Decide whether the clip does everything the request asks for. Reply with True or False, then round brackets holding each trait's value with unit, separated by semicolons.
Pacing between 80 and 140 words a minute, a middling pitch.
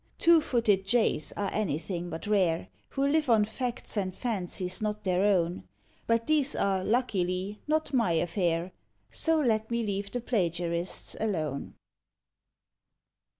False (135 wpm; 205 Hz)